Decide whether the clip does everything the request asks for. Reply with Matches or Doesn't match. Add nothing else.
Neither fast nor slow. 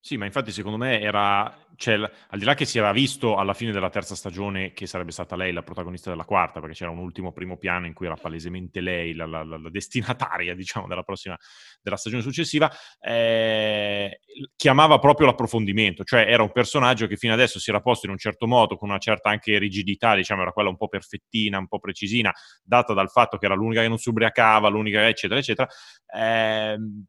Doesn't match